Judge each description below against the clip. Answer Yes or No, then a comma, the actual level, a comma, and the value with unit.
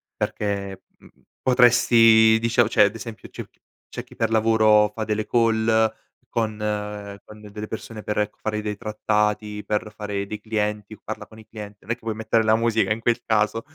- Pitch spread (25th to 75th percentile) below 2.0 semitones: Yes, narrow, 1.2 semitones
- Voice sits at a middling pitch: No, low, 110 Hz